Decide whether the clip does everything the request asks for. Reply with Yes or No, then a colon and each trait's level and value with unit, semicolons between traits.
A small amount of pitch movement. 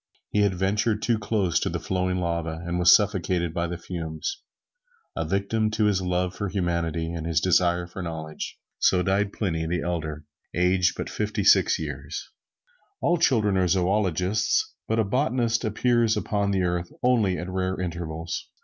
No: average, 3.3 semitones